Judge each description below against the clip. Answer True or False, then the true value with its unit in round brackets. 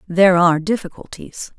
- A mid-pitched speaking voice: True (180 Hz)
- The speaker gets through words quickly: False (115 wpm)